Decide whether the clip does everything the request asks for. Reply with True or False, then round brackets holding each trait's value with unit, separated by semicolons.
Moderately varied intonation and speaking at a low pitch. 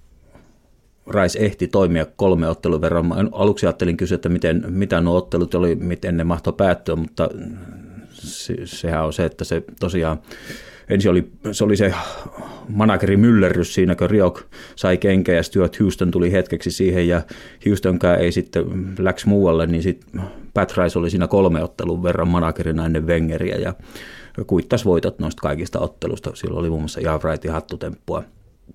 False (2.3 semitones; 90 Hz)